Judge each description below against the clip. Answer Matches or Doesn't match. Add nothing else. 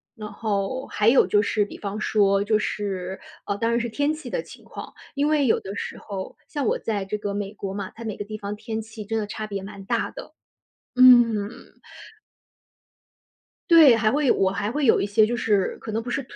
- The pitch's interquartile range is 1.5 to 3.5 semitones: Matches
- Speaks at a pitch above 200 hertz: Matches